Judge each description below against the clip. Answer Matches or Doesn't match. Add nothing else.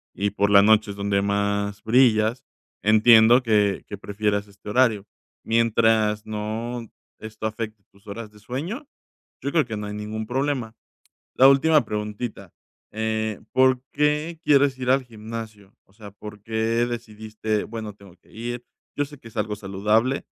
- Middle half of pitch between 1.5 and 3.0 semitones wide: Matches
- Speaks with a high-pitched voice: Doesn't match